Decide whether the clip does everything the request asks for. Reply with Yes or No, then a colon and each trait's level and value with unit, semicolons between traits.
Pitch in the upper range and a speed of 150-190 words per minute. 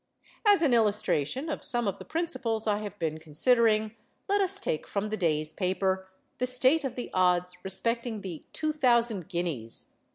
Yes: high, 215 Hz; average, 170 wpm